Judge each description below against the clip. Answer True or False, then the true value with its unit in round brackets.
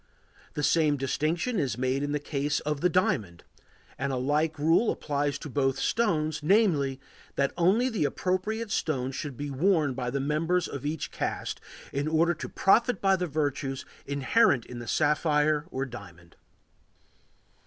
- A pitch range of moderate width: True (4.0 semitones)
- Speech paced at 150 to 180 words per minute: True (160 wpm)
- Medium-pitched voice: True (150 Hz)